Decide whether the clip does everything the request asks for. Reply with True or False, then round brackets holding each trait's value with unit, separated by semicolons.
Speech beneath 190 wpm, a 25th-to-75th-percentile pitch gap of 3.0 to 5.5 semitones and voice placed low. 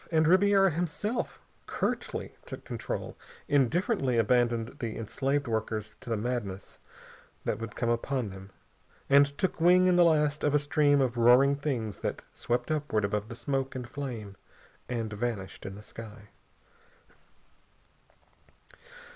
True (140 wpm; 4.9 semitones; 125 Hz)